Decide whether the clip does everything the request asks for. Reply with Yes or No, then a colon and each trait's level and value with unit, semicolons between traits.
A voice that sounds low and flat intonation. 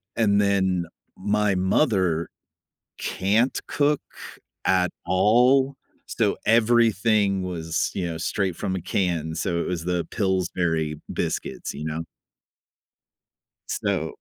No: very low, 95 Hz; average, 3.6 semitones